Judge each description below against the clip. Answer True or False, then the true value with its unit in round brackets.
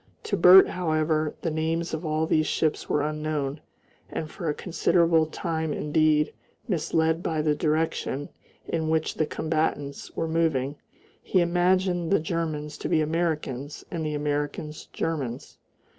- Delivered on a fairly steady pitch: True (1.6 semitones)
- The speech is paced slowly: False (145 wpm)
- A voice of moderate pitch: True (155 Hz)